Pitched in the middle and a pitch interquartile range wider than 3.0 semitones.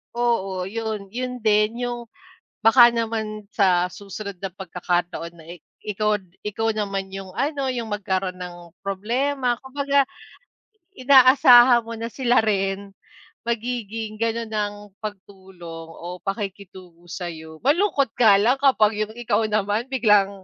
No: high, 215 Hz; average, 3.9 semitones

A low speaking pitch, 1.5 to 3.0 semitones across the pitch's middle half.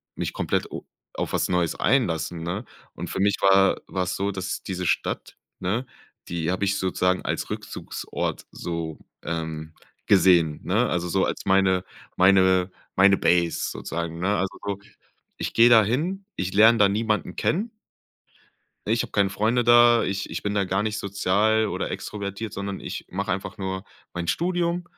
Yes: very low, 95 Hz; average, 2.7 semitones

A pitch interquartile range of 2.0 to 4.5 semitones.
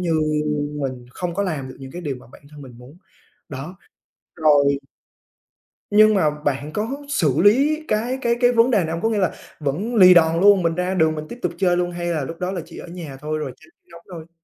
No: average, 5.1 semitones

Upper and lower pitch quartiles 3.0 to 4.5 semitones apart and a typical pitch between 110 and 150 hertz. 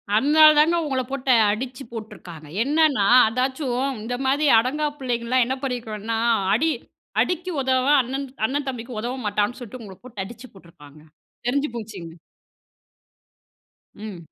No: average, 4.0 semitones; very high, 250 Hz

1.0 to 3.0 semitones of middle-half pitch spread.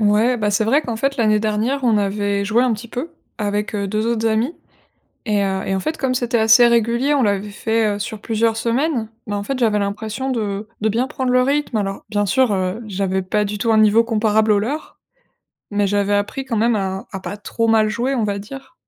Yes: average, 2.7 semitones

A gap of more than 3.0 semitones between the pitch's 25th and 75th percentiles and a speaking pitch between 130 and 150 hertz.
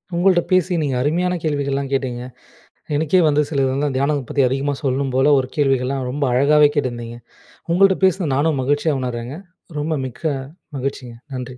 No: average, 2.7 semitones; medium, 140 Hz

